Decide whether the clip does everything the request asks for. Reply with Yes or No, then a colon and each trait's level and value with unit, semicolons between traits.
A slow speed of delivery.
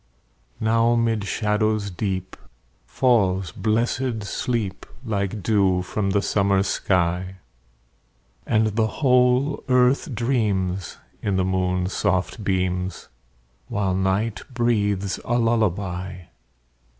Yes: slow, 100 wpm